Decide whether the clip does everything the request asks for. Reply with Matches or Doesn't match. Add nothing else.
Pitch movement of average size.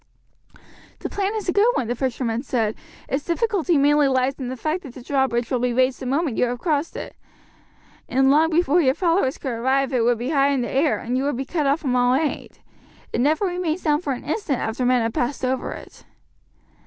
Matches